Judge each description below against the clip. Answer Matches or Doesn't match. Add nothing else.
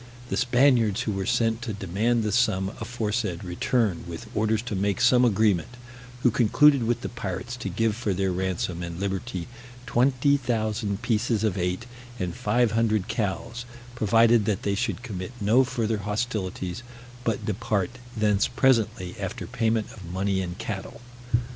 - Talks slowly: Doesn't match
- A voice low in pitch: Matches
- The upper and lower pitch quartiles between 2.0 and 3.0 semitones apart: Doesn't match